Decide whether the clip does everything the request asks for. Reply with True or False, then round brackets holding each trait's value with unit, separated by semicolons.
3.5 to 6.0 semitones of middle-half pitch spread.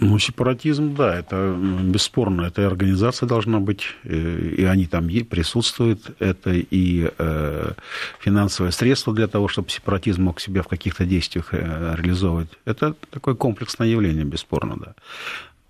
True (4.3 semitones)